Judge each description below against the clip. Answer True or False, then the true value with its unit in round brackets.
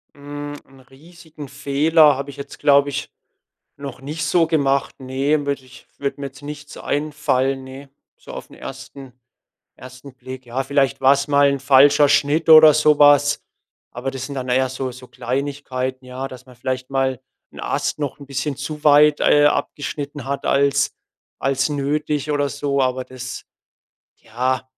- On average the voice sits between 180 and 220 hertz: False (140 Hz)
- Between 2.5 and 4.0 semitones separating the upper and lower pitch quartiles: False (1.9 semitones)